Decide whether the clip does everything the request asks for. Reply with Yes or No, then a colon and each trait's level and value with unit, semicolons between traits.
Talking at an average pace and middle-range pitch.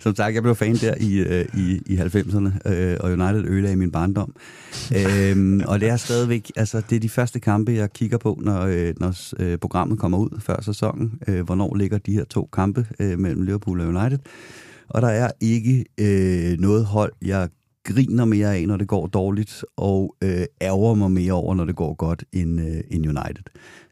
No: average, 175 wpm; low, 100 Hz